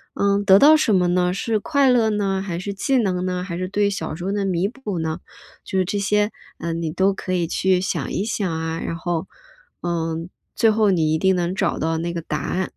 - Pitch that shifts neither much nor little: Yes, average, 3.0 semitones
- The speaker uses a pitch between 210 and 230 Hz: No, medium, 185 Hz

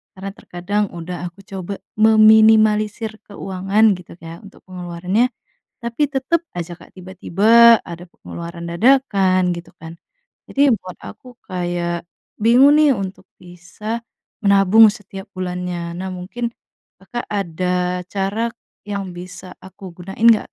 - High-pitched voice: Yes, high, 195 Hz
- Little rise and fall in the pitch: No, average, 3.5 semitones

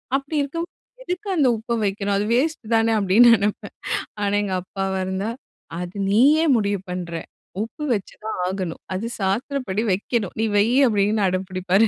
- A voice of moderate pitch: No, high, 205 Hz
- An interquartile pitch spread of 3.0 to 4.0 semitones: Yes, average, 3.6 semitones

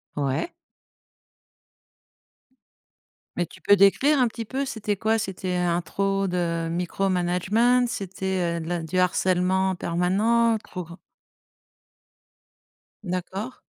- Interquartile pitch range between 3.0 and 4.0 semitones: Yes, average, 3.4 semitones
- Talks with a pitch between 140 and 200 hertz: Yes, high, 190 Hz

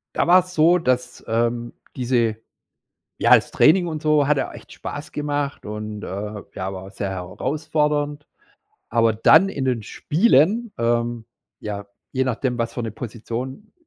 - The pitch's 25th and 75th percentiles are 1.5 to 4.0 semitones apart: No, average, 4.7 semitones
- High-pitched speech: No, low, 130 Hz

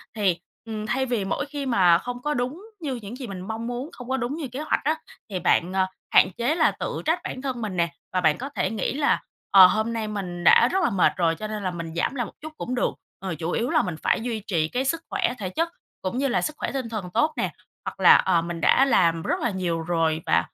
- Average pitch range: No, wide, 6.5 semitones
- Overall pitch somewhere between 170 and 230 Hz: Yes, high, 220 Hz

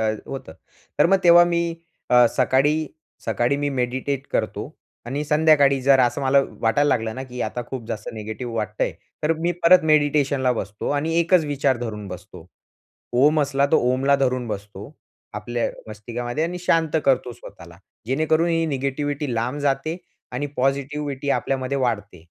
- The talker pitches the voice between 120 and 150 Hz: Yes, low, 135 Hz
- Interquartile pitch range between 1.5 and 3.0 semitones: No, average, 3.7 semitones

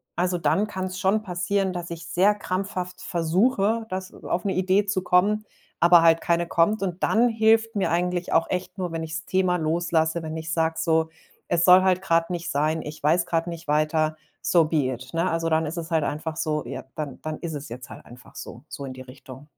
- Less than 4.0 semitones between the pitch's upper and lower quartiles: Yes, average, 2.7 semitones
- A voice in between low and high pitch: Yes, medium, 170 Hz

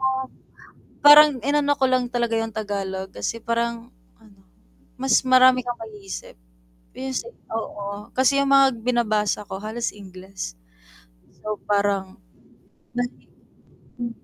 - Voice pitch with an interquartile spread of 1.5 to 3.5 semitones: No, average, 4.0 semitones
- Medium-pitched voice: No, high, 230 Hz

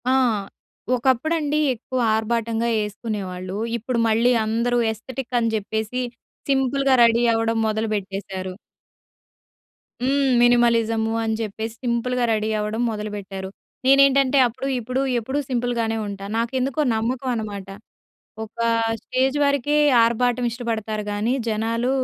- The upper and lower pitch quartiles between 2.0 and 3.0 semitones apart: Yes, narrow, 2.6 semitones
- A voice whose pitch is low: No, high, 230 Hz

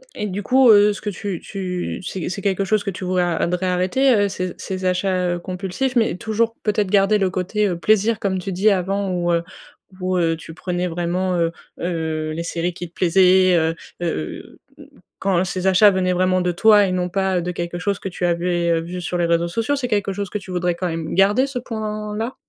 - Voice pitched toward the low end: No, medium, 185 Hz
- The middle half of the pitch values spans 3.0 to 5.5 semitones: No, narrow, 2.5 semitones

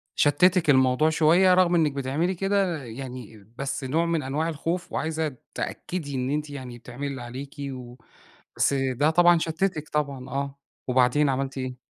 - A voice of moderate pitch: Yes, medium, 145 Hz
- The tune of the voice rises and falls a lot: No, average, 3.8 semitones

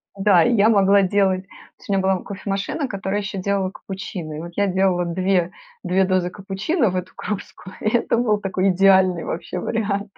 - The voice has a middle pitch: No, high, 195 Hz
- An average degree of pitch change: No, narrow, 1.5 semitones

